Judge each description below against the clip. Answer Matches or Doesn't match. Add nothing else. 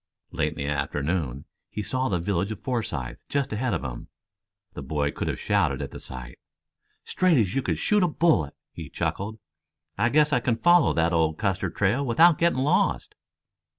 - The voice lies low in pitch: Matches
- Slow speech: Doesn't match